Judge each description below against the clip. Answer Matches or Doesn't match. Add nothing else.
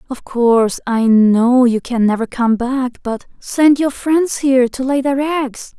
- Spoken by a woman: Matches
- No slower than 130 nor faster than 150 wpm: Doesn't match